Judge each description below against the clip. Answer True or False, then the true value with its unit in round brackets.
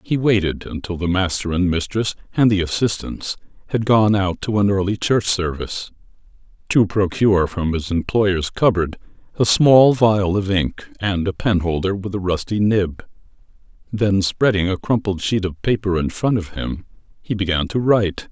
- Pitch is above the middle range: False (100 Hz)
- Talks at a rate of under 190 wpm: True (165 wpm)